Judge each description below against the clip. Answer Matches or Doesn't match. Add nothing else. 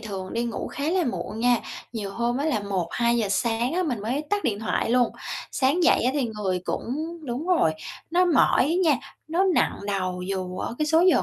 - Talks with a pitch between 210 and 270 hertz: Matches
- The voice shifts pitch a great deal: Matches